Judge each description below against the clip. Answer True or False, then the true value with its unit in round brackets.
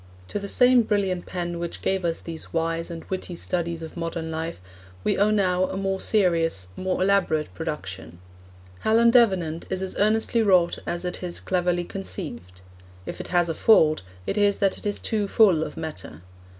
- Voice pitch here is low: False (180 Hz)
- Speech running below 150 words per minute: False (185 wpm)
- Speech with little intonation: False (3.3 semitones)